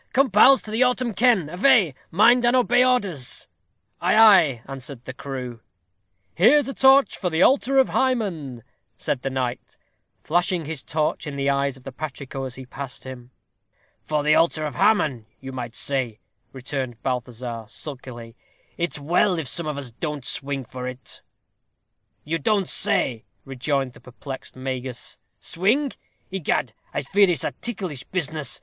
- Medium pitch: Yes, medium, 145 Hz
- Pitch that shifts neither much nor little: No, wide, 6.9 semitones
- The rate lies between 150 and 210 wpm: Yes, average, 160 wpm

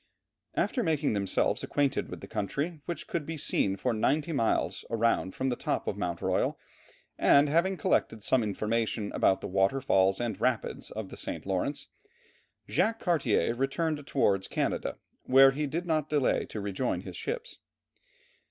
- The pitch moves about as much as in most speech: No, wide, 6.5 semitones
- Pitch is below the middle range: Yes, low, 130 Hz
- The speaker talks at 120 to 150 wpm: No, average, 160 wpm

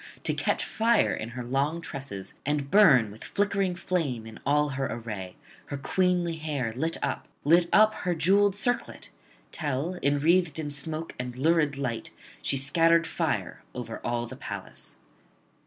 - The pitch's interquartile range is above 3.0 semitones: Yes, average, 5.0 semitones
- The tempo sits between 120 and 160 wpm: Yes, average, 155 wpm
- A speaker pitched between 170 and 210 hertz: No, medium, 150 Hz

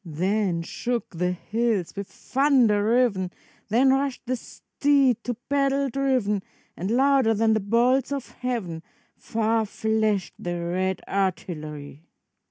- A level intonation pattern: No, average, 5.3 semitones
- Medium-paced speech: No, slow, 125 wpm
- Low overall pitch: No, high, 220 Hz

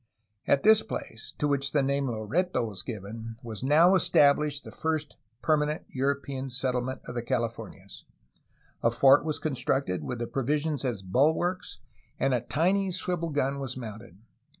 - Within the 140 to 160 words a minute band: Yes, average, 155 wpm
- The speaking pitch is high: No, low, 135 Hz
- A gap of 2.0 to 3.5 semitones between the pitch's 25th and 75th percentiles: No, average, 4.3 semitones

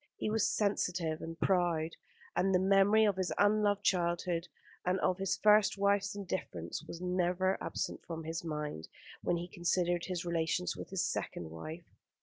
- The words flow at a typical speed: Yes, average, 160 wpm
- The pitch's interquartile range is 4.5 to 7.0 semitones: No, average, 2.9 semitones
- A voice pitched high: No, medium, 180 Hz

